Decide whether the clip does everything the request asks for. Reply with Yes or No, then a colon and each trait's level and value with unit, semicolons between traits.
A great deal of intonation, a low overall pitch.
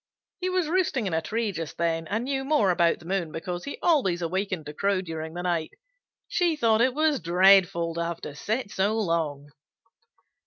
No: wide, 5.8 semitones; medium, 185 Hz